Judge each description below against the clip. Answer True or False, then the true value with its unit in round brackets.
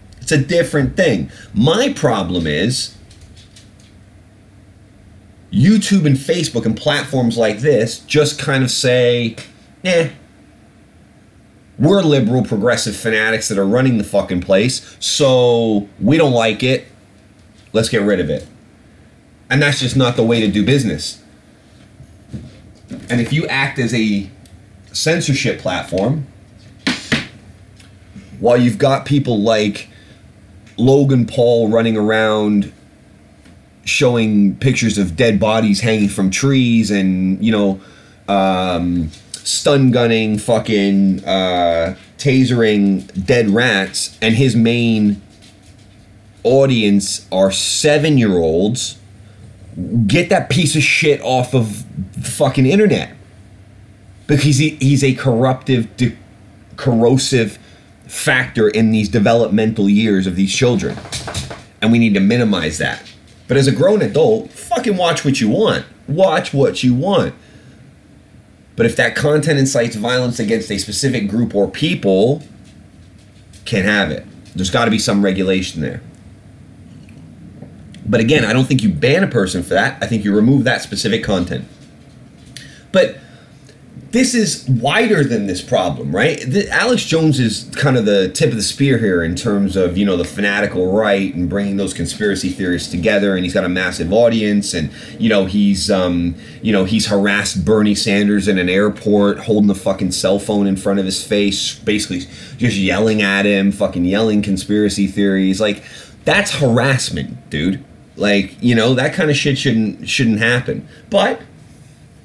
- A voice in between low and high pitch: False (110 Hz)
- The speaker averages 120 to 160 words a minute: True (140 wpm)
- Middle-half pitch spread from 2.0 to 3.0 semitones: False (4.3 semitones)